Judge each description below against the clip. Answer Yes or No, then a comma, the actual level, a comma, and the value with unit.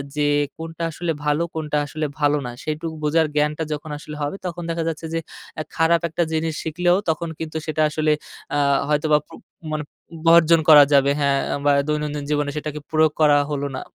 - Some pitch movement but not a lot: No, narrow, 1.6 semitones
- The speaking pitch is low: No, medium, 155 Hz